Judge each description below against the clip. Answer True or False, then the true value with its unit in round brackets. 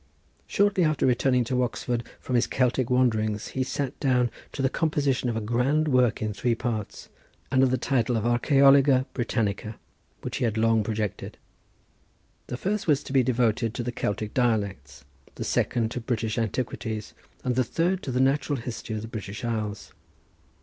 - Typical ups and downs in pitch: True (3.0 semitones)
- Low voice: True (120 Hz)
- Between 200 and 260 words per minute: False (170 wpm)